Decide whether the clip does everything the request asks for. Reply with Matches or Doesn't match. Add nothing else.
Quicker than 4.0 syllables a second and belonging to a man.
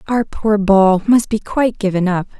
Doesn't match